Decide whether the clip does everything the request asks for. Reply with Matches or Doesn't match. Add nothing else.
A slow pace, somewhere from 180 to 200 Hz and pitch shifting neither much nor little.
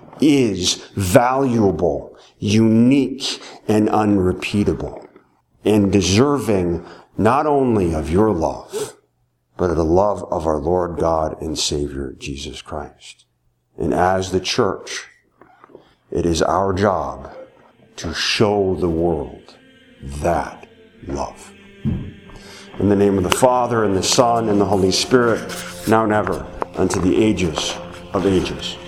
Doesn't match